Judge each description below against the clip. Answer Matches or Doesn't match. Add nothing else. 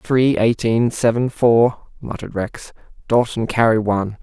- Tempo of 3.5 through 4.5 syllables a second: Matches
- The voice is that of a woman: Doesn't match